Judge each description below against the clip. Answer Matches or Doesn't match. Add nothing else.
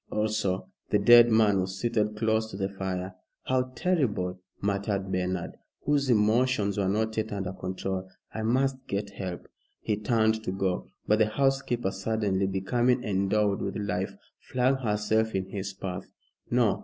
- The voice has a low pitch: Matches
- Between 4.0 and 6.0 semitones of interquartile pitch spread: Doesn't match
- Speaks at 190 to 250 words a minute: Doesn't match